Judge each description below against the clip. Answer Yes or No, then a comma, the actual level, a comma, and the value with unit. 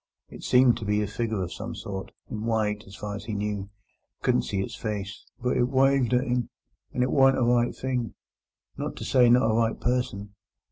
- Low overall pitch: Yes, low, 115 Hz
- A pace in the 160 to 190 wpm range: No, average, 200 wpm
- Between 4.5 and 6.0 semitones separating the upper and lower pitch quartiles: No, average, 3.3 semitones